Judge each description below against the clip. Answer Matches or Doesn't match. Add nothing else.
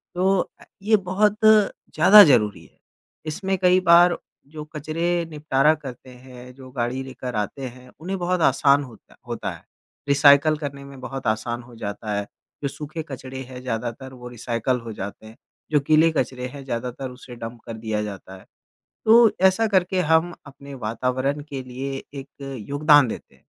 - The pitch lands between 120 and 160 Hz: Matches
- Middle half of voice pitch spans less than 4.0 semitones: Doesn't match